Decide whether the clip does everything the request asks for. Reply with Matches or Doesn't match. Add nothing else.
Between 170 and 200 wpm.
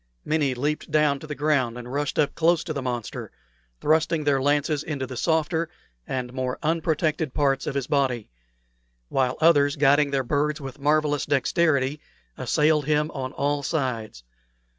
Doesn't match